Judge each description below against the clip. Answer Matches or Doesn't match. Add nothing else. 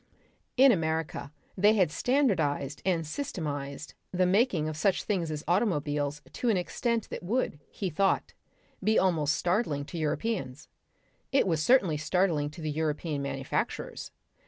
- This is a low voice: Doesn't match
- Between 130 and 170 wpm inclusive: Matches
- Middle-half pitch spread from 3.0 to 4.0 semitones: Doesn't match